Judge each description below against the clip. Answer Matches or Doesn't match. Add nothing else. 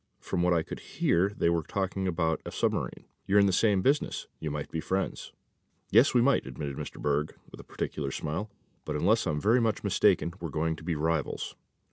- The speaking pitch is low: Matches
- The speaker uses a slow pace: Doesn't match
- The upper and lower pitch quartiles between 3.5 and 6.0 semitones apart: Matches